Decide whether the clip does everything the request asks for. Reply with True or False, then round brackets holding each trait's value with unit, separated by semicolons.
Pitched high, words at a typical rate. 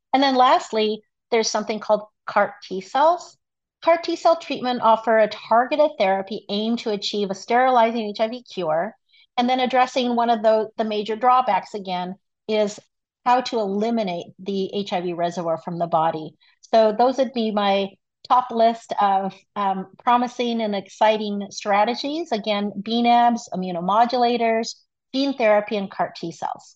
True (220 Hz; 150 wpm)